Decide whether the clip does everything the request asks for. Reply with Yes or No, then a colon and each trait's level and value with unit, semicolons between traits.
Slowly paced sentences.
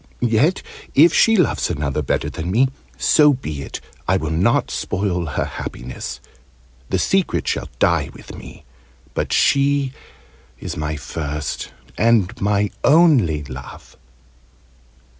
Yes: slow, 125 wpm